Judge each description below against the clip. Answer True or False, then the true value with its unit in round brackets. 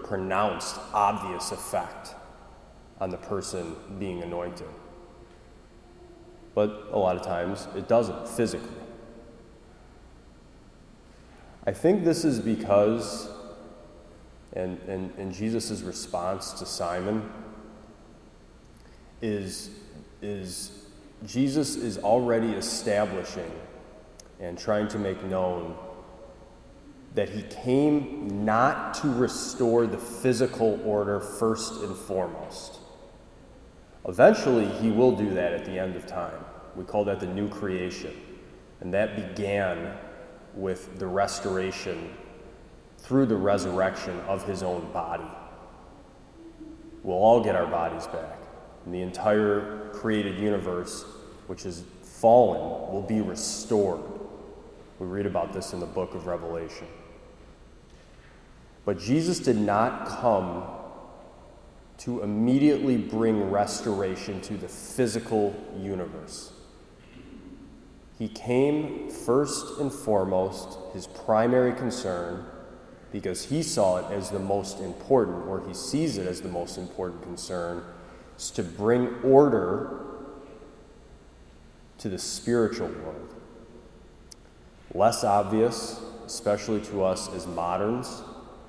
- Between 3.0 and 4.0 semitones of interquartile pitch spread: True (3.6 semitones)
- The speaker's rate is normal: False (110 wpm)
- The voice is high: False (100 Hz)